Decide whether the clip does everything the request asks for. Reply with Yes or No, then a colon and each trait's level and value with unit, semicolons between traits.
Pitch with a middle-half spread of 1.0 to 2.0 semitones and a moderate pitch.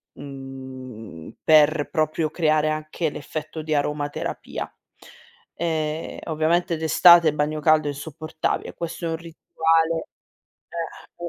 Yes: narrow, 1.7 semitones; medium, 155 Hz